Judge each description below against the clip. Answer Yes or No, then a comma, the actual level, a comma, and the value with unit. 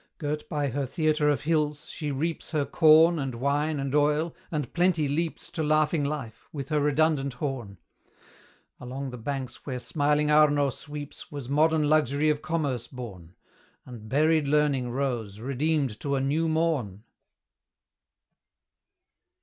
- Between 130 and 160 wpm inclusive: Yes, average, 140 wpm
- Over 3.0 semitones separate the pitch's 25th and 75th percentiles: No, narrow, 2.6 semitones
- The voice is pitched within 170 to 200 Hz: No, medium, 145 Hz